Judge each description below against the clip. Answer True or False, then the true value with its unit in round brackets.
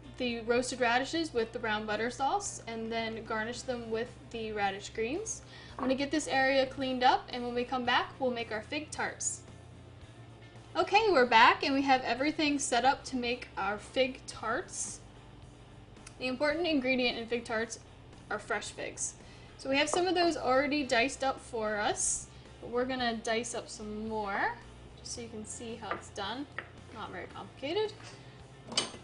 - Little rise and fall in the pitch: False (3.4 semitones)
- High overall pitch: True (245 Hz)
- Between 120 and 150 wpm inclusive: False (180 wpm)